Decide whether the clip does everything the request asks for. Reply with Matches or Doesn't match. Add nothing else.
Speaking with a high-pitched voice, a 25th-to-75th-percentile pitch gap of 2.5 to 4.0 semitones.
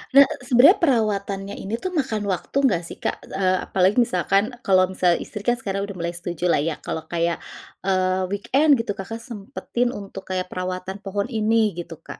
Matches